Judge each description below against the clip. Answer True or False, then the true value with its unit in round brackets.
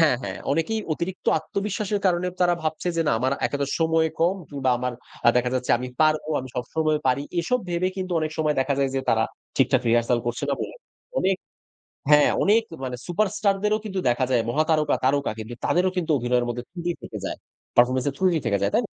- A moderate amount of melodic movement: False (5.8 semitones)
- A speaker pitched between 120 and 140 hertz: False (155 Hz)